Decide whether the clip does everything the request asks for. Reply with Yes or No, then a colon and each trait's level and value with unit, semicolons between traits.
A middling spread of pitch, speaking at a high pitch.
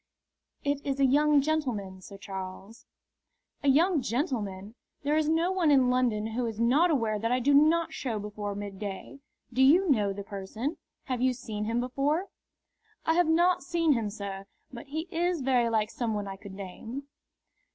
No: wide, 6.2 semitones; very high, 250 Hz